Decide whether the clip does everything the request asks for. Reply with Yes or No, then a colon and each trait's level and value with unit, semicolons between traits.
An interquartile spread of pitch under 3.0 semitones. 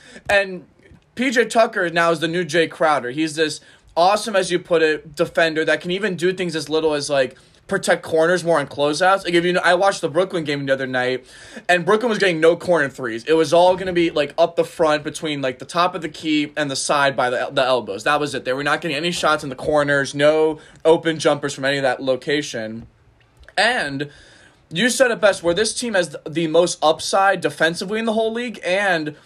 No: average, 3.5 semitones